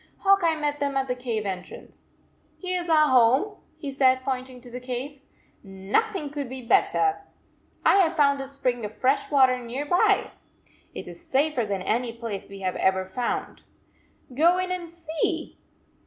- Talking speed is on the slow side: No, average, 185 wpm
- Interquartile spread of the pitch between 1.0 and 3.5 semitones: No, average, 4.7 semitones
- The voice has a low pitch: No, very high, 265 Hz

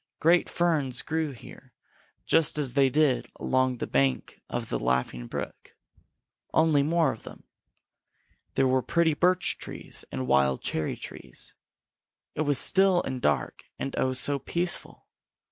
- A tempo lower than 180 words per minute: Yes, average, 145 wpm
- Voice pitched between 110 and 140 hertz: Yes, low, 135 Hz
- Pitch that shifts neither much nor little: Yes, average, 4.8 semitones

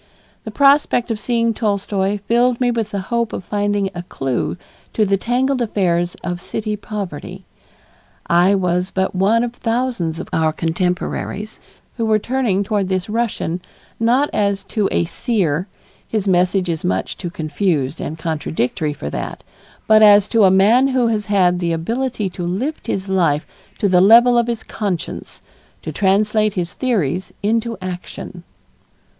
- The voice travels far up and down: No, average, 4.3 semitones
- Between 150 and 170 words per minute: Yes, average, 160 wpm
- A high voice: Yes, high, 200 Hz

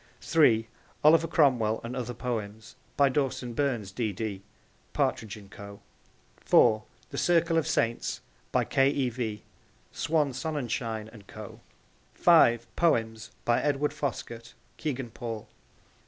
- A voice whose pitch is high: No, low, 120 Hz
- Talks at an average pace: No, slow, 125 wpm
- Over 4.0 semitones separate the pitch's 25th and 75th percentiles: Yes, average, 4.6 semitones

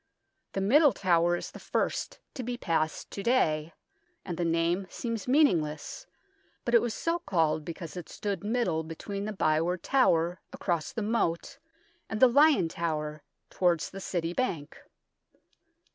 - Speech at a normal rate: Yes, average, 155 wpm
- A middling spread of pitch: No, wide, 6.0 semitones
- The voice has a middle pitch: Yes, medium, 180 Hz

